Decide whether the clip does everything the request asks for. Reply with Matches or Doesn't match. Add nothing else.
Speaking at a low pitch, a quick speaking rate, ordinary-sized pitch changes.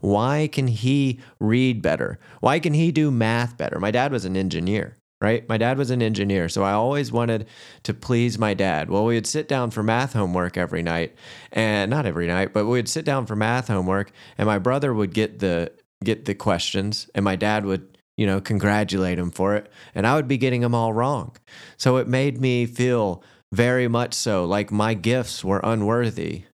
Matches